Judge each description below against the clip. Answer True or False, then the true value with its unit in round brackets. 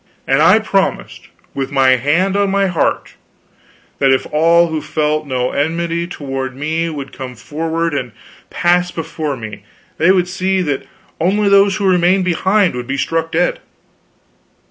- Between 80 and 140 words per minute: False (155 wpm)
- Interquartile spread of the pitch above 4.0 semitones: True (4.4 semitones)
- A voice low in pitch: False (165 Hz)